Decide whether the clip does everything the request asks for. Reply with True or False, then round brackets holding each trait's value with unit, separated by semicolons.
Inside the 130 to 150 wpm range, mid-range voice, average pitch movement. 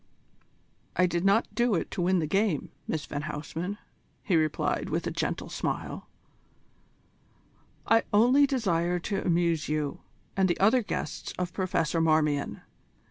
True (140 wpm; 175 Hz; 4.1 semitones)